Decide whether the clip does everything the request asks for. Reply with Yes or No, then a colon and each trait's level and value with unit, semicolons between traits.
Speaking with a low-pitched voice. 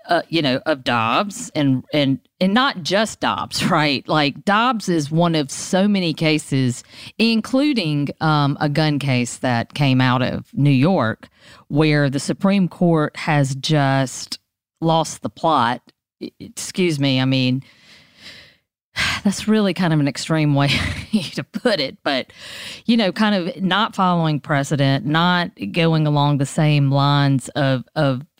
No: medium, 150 Hz